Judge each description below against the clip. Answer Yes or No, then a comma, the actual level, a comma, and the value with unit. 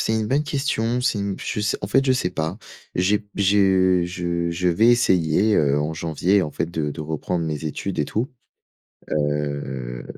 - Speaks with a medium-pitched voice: No, very low, 90 Hz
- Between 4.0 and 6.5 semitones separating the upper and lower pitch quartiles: Yes, average, 5.1 semitones